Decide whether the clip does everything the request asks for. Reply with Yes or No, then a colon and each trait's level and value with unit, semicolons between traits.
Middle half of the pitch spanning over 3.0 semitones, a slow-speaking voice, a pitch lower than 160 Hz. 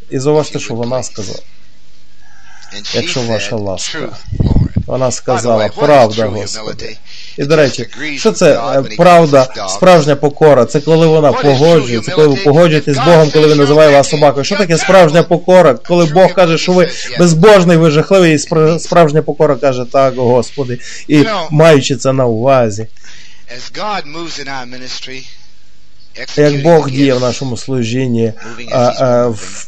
No: average, 4.6 semitones; average, 135 wpm; medium, 140 Hz